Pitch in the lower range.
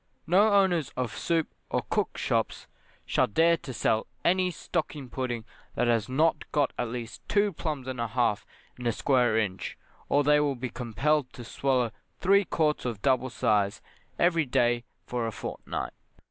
Yes: low, 130 Hz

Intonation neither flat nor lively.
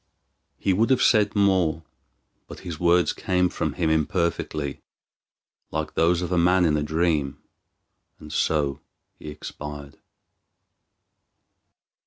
Yes: average, 3.0 semitones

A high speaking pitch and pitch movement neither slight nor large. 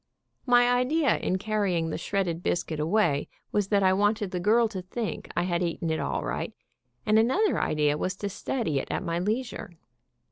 Yes: high, 195 Hz; average, 4.4 semitones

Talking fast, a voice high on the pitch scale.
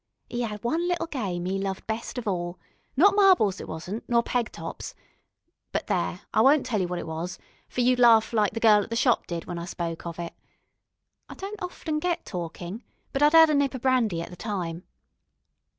Yes: fast, 215 wpm; high, 220 Hz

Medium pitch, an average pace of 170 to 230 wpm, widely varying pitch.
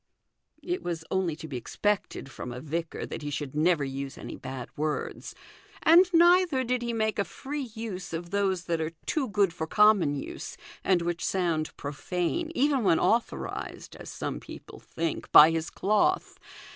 Yes: medium, 175 Hz; average, 175 wpm; wide, 6.6 semitones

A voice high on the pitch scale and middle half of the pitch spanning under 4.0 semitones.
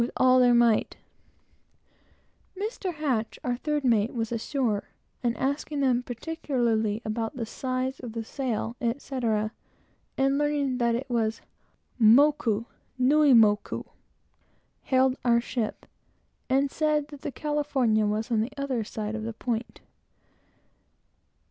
Yes: high, 245 Hz; average, 3.6 semitones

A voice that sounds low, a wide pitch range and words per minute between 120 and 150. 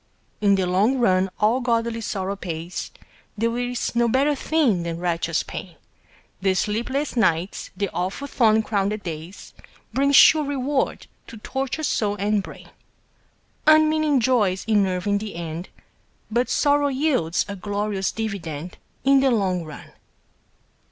No: high, 210 Hz; wide, 5.8 semitones; average, 140 wpm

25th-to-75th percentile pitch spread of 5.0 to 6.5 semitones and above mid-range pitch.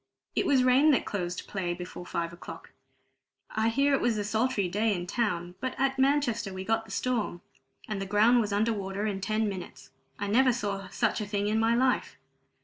No: average, 3.7 semitones; high, 215 Hz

